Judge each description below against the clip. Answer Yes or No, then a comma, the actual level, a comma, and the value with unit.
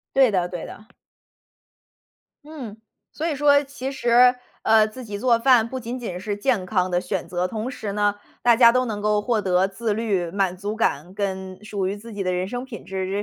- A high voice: Yes, high, 210 Hz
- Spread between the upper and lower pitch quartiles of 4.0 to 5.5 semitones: Yes, average, 4.3 semitones